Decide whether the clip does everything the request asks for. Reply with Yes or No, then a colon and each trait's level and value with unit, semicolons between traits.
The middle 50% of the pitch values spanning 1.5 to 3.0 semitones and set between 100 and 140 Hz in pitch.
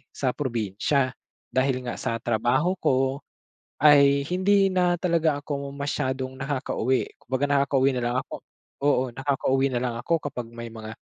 Yes: narrow, 2.5 semitones; low, 135 Hz